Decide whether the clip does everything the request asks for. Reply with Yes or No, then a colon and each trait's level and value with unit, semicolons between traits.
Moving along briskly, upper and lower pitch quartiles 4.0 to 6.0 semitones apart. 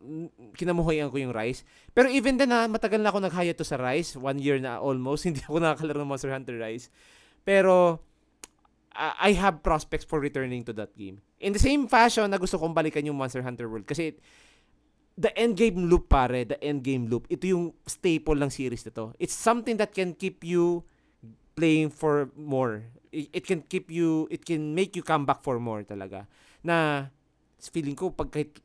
Yes: fast, 190 wpm; average, 4.9 semitones